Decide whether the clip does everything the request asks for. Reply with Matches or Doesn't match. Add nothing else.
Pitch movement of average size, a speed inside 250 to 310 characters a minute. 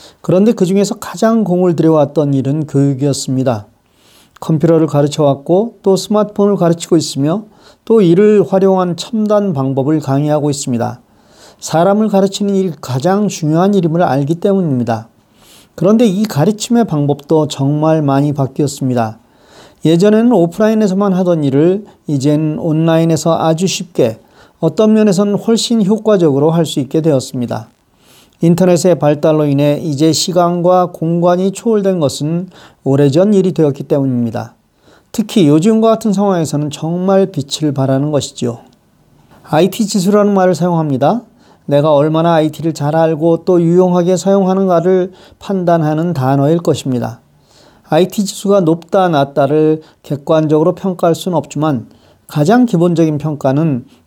Doesn't match